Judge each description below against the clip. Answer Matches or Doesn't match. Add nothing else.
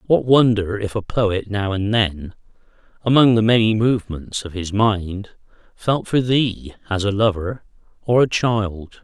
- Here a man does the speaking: Matches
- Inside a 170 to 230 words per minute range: Doesn't match